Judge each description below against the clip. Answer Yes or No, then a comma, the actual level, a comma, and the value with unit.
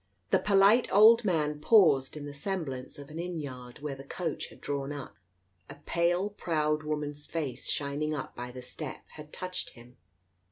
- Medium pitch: Yes, medium, 150 Hz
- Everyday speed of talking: Yes, average, 175 wpm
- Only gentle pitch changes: No, average, 3.9 semitones